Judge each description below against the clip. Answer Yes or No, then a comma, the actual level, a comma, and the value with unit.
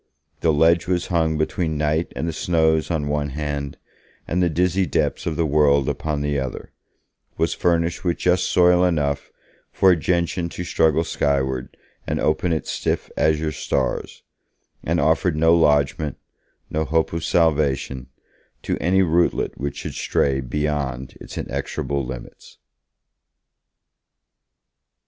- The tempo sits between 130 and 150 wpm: Yes, average, 140 wpm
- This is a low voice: Yes, very low, 80 Hz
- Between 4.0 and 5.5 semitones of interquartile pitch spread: No, average, 2.8 semitones